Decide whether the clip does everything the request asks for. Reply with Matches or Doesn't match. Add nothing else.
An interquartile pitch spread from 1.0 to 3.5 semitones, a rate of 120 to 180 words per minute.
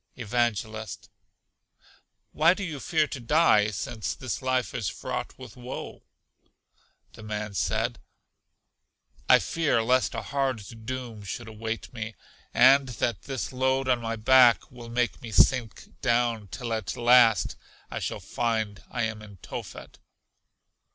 Matches